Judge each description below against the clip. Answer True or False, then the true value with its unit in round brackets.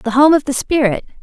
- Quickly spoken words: True (245 wpm)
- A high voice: True (265 Hz)